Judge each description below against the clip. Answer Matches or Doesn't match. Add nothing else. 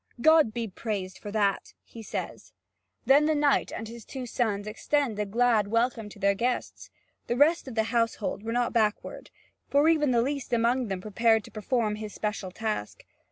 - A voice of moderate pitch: Doesn't match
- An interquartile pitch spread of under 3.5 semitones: Matches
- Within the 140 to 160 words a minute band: Doesn't match